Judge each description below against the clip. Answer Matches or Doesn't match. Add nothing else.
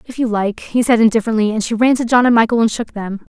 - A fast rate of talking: Matches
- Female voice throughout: Matches